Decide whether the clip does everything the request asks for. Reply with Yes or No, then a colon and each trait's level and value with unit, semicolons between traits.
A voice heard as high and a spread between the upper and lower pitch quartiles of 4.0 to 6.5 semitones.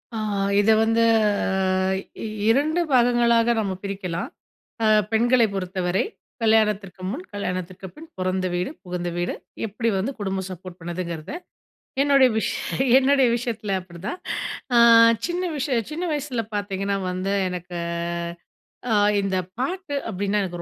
Yes: high, 205 Hz; average, 4.7 semitones